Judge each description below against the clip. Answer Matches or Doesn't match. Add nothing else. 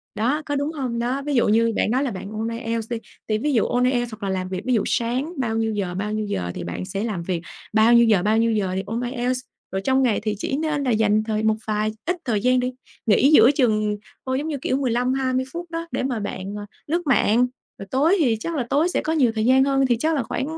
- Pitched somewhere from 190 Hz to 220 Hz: Doesn't match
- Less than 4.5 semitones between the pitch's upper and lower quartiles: Matches